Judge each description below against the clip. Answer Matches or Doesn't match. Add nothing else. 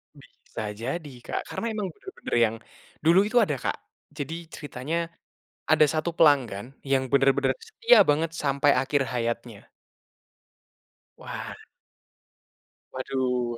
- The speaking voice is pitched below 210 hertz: Matches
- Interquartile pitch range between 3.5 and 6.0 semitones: Matches